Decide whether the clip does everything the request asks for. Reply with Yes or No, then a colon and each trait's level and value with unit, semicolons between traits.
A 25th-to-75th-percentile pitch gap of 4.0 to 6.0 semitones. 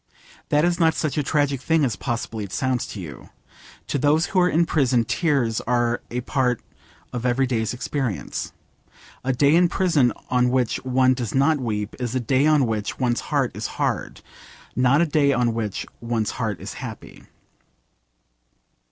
No: average, 3.6 semitones